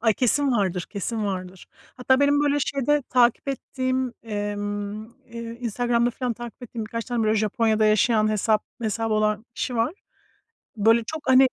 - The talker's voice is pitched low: No, high, 230 Hz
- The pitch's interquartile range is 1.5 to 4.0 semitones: Yes, average, 3.1 semitones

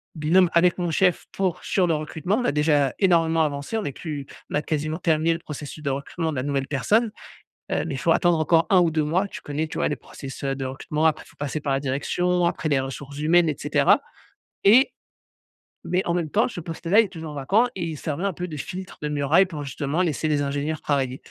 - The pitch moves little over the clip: No, average, 3.6 semitones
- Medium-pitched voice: Yes, medium, 155 Hz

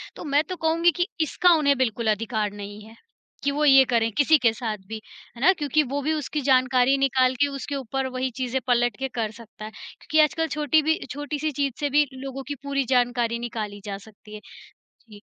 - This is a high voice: Yes, very high, 265 Hz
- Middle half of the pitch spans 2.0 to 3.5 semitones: No, average, 4.3 semitones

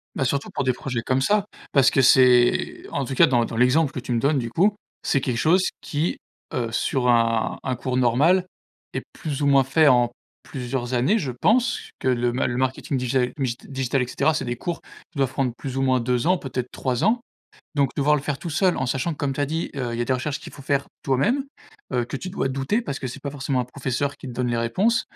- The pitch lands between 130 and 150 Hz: Yes, low, 135 Hz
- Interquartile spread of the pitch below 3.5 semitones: Yes, average, 2.8 semitones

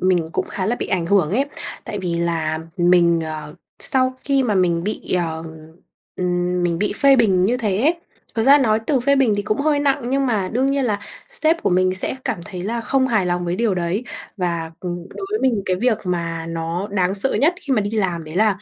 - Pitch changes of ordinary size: No, wide, 6.1 semitones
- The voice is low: No, high, 195 Hz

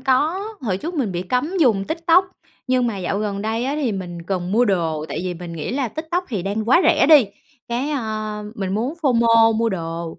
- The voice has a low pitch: No, high, 225 Hz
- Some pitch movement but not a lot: No, wide, 6.1 semitones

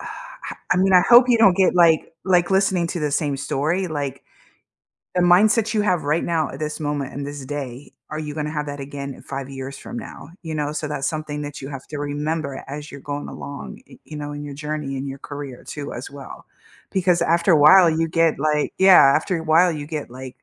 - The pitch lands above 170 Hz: No, medium, 150 Hz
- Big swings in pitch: No, average, 3.3 semitones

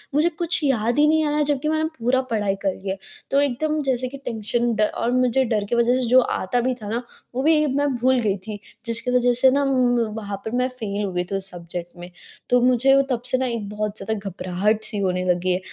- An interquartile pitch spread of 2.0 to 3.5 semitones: No, average, 4.1 semitones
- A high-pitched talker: Yes, high, 240 Hz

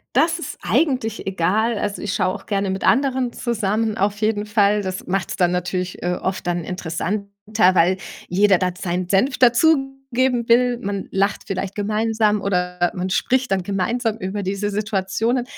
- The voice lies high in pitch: Yes, high, 200 Hz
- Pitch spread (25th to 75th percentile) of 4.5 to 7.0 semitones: No, average, 3.4 semitones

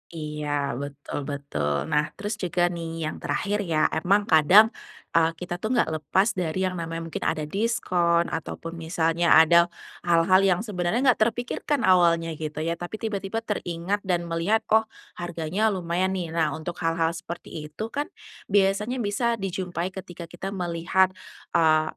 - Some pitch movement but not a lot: Yes, average, 3.1 semitones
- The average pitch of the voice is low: No, medium, 175 Hz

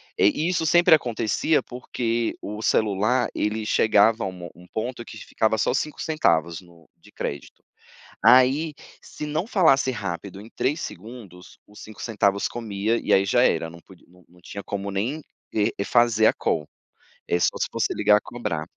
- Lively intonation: No, average, 4.3 semitones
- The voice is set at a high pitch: No, low, 110 Hz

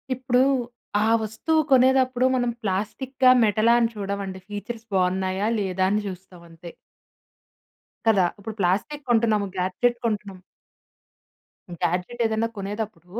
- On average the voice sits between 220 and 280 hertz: No, high, 210 Hz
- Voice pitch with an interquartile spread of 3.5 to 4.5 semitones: Yes, average, 4.0 semitones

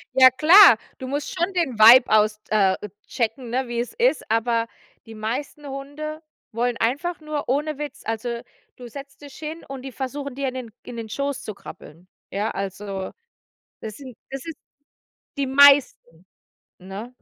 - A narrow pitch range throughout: No, average, 4.2 semitones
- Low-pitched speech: No, very high, 255 Hz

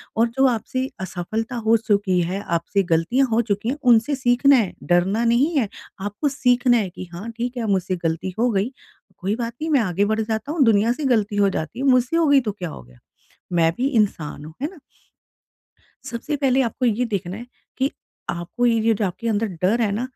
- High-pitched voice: Yes, high, 225 Hz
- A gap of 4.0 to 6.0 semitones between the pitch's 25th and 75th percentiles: Yes, average, 4.3 semitones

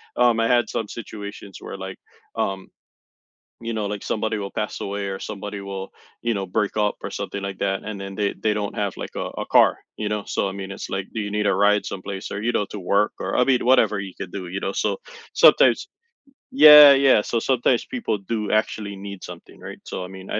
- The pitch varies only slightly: Yes, narrow, 2.0 semitones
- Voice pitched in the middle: No, low, 105 Hz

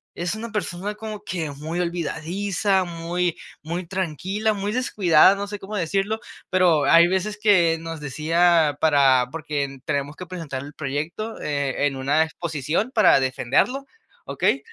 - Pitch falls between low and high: Yes, medium, 170 Hz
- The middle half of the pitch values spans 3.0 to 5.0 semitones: Yes, average, 4.7 semitones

